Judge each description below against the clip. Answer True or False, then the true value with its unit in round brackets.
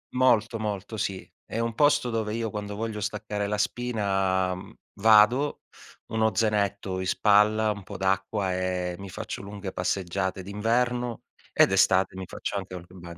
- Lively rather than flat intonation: False (2.8 semitones)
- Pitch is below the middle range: True (105 Hz)